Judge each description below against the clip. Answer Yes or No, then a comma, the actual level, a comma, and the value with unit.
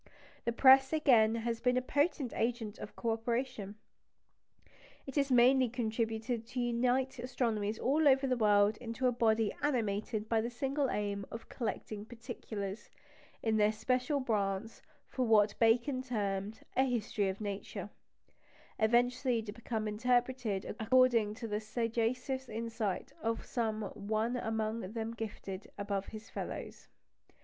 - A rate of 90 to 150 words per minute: Yes, average, 140 wpm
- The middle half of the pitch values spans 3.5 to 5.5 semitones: No, average, 2.7 semitones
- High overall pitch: Yes, high, 230 Hz